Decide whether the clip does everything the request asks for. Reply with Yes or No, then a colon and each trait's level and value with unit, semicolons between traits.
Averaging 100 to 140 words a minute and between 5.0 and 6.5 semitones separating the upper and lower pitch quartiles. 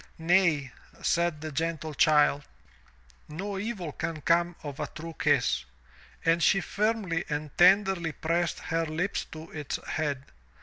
No: slow, 135 wpm; narrow, 2.5 semitones